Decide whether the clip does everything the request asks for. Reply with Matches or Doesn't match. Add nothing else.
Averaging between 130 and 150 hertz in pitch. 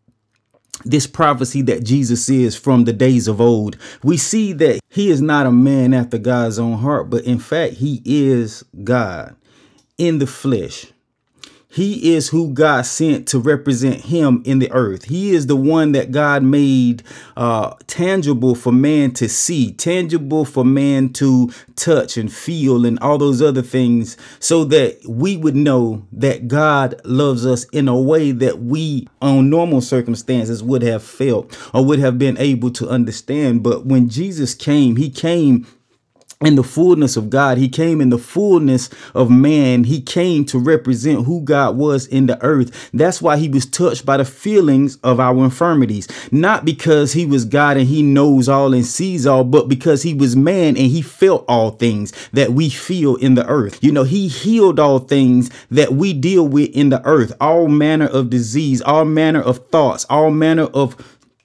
Matches